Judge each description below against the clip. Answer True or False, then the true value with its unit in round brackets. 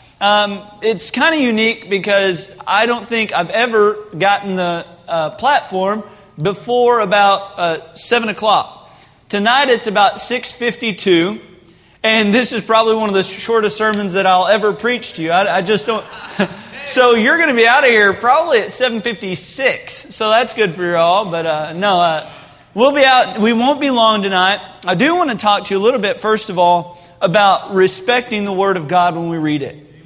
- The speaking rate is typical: True (195 wpm)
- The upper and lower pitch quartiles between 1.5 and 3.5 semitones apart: False (3.9 semitones)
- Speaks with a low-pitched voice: False (205 Hz)